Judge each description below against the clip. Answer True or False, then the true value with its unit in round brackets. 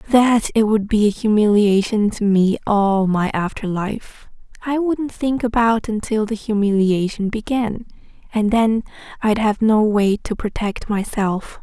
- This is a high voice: True (215 Hz)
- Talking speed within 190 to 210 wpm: False (150 wpm)